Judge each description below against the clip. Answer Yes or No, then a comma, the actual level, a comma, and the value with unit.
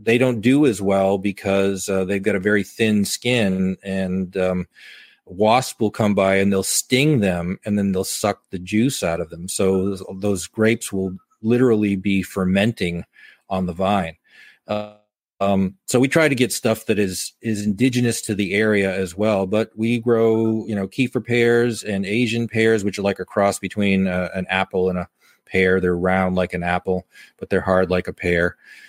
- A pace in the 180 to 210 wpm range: Yes, average, 195 wpm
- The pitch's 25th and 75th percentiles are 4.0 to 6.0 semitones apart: No, average, 2.8 semitones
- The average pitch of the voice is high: No, low, 100 Hz